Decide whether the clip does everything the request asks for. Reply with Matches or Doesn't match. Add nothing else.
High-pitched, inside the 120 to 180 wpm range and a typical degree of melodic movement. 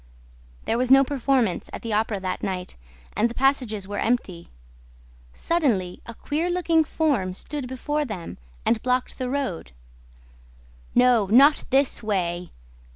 Doesn't match